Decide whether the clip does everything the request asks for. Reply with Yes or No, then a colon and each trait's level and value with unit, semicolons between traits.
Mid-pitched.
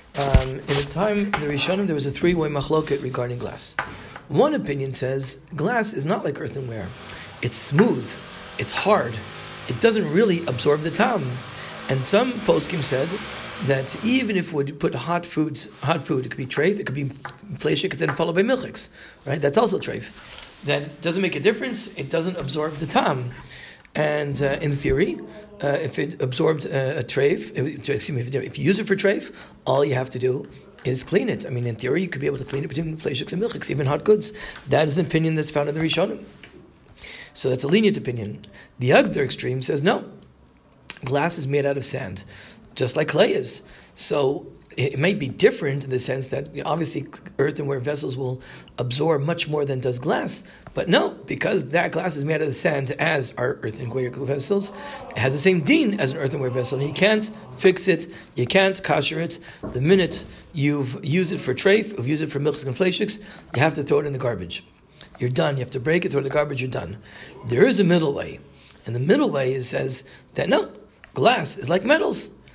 Yes: medium, 145 Hz